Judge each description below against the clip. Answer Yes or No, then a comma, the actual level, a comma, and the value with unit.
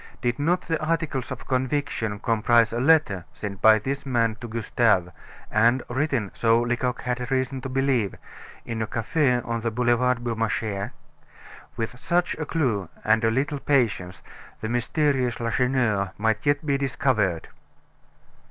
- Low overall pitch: Yes, low, 120 Hz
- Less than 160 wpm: Yes, average, 145 wpm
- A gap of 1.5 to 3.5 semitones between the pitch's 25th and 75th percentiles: Yes, average, 3.2 semitones